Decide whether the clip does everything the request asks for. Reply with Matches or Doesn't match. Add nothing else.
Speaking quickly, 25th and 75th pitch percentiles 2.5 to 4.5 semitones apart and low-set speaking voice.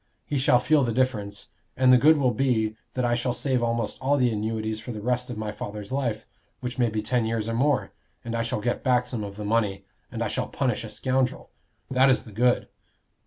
Matches